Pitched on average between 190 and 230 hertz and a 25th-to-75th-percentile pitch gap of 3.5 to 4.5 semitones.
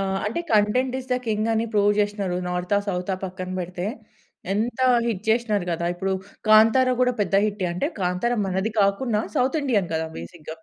Yes: high, 205 Hz; average, 3.8 semitones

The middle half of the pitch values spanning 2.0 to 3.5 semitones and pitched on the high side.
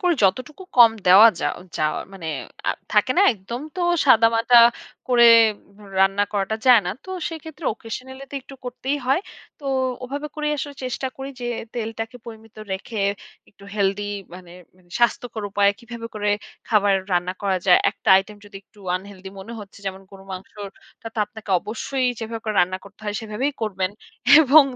No: average, 4.2 semitones; high, 220 Hz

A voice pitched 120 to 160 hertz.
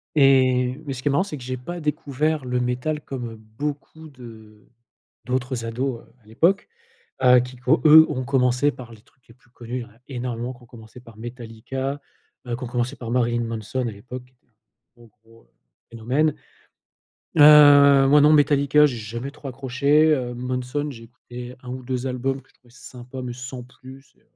Yes: low, 125 Hz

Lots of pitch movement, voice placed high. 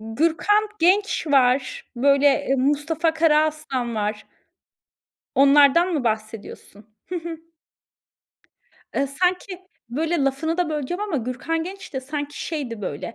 No: average, 4.3 semitones; very high, 295 Hz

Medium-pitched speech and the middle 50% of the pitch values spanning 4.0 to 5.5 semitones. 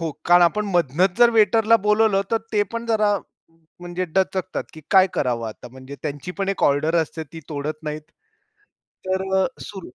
Yes: medium, 180 Hz; average, 5.2 semitones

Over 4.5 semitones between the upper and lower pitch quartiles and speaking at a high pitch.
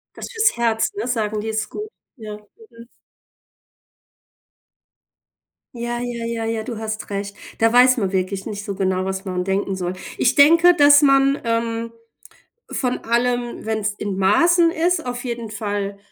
No: average, 3.6 semitones; high, 230 Hz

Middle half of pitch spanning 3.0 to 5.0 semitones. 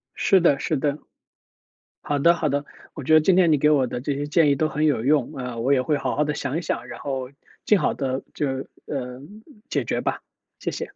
No: narrow, 2.6 semitones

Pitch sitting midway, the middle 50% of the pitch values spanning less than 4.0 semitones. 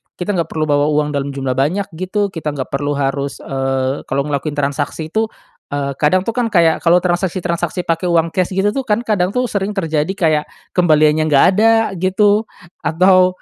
No: medium, 165 Hz; average, 4.6 semitones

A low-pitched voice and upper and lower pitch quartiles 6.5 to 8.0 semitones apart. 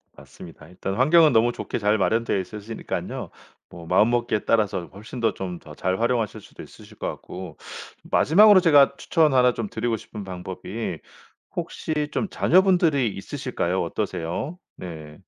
Yes: low, 115 Hz; wide, 6.8 semitones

